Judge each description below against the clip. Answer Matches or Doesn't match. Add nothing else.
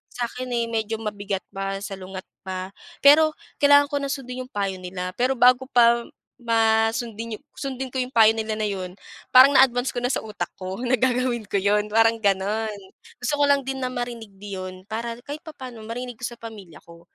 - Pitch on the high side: Matches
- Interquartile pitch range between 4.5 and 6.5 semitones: Doesn't match